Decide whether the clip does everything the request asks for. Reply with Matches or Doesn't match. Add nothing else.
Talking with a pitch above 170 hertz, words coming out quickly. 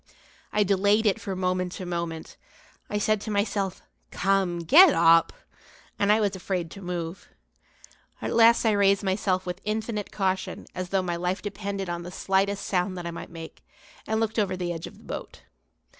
Doesn't match